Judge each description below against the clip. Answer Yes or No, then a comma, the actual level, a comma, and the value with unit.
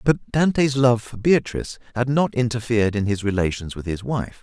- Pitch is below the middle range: Yes, low, 115 Hz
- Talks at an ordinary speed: Yes, average, 190 wpm